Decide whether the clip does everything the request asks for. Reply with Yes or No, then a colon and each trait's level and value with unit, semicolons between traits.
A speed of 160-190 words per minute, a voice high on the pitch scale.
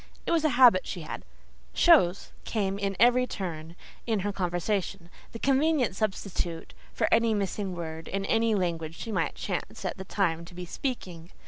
Yes: average, 175 wpm; high, 195 Hz